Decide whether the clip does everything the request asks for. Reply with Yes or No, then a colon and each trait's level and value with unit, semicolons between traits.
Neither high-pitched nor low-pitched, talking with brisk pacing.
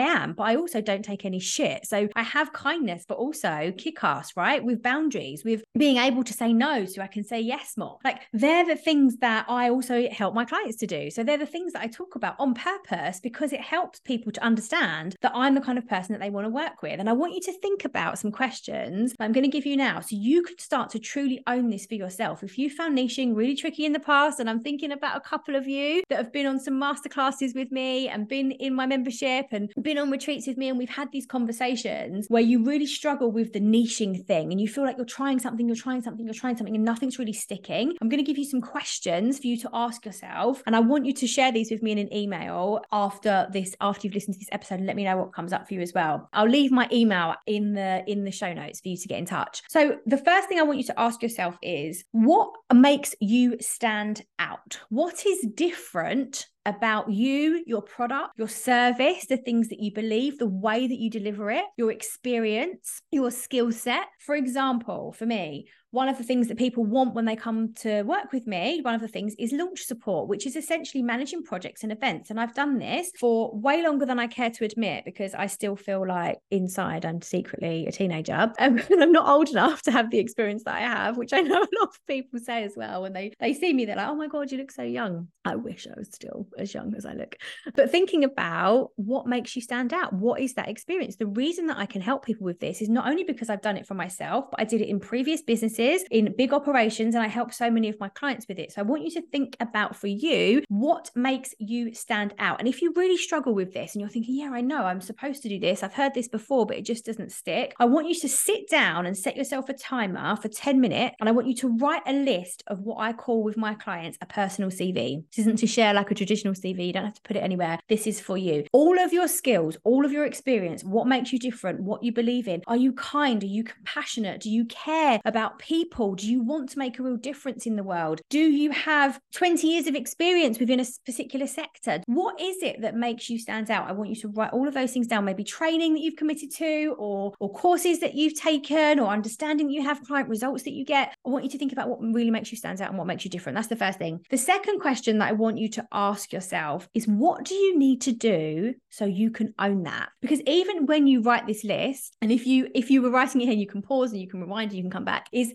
No: high, 240 Hz; fast, 260 wpm